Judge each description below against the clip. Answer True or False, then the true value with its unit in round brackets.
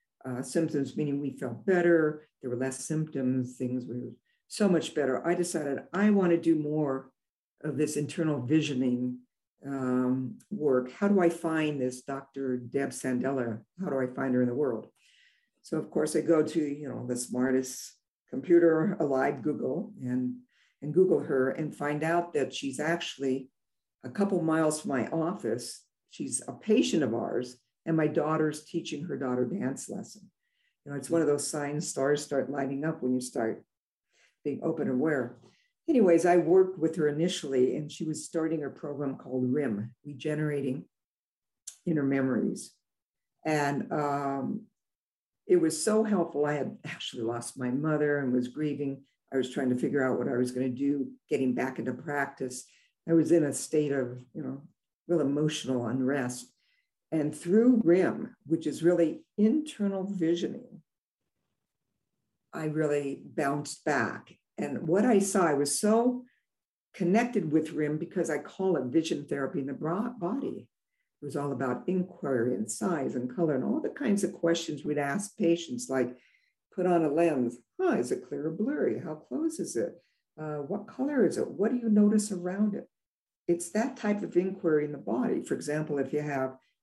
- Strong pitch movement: False (4.7 semitones)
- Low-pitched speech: False (150 Hz)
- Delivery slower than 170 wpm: False (175 wpm)